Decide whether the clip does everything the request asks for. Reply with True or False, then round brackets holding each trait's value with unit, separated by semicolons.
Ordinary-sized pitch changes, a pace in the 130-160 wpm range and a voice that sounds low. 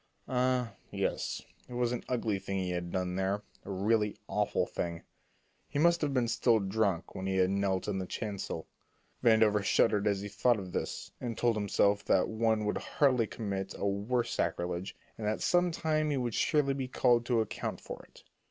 False (4.1 semitones; 190 wpm; 105 Hz)